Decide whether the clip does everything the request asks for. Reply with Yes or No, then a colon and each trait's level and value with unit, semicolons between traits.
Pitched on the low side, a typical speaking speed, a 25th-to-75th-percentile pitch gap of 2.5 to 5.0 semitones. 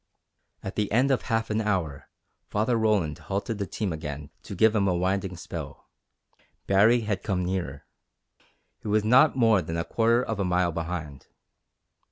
Yes: low, 100 Hz; average, 170 wpm; average, 4.1 semitones